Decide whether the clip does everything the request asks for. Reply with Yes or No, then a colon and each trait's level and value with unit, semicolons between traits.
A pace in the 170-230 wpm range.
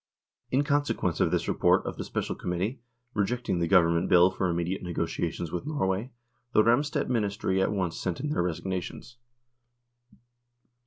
No: average, 155 wpm